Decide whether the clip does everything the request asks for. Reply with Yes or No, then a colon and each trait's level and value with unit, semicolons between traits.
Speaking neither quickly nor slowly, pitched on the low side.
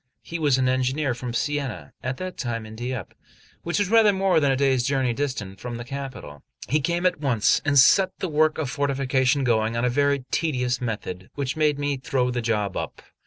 No: fast, 210 wpm; low, 130 Hz